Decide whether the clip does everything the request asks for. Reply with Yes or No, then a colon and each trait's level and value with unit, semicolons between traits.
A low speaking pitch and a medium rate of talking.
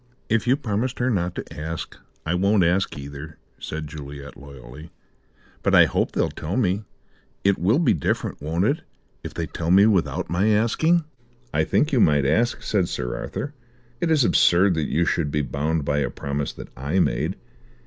Yes: very low, 85 Hz; average, 185 wpm